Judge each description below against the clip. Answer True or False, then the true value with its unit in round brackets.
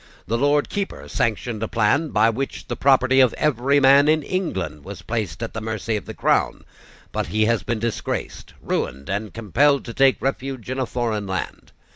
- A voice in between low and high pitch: False (115 Hz)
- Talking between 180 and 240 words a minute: True (190 wpm)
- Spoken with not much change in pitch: False (4.1 semitones)